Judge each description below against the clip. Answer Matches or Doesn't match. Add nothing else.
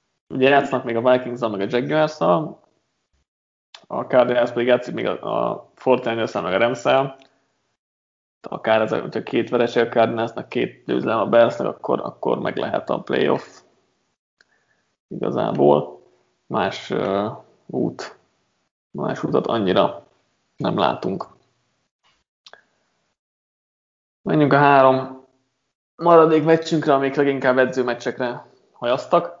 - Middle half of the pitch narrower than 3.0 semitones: Matches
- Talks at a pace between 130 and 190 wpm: Doesn't match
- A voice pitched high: Doesn't match